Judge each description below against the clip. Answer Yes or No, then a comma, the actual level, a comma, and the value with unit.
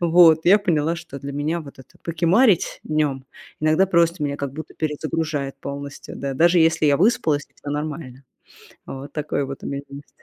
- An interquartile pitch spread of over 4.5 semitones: No, average, 2.9 semitones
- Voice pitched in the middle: Yes, medium, 155 Hz